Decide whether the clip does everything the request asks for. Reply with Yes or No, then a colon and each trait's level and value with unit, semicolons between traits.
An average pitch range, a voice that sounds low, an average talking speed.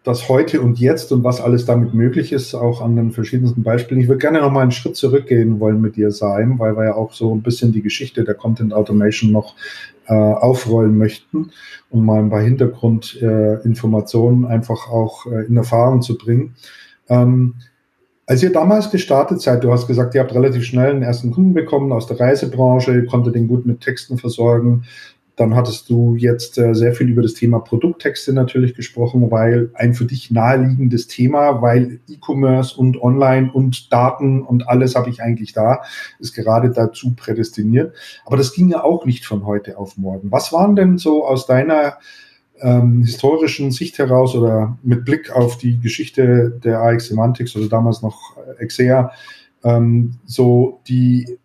No: narrow, 2.2 semitones; low, 120 Hz; average, 180 wpm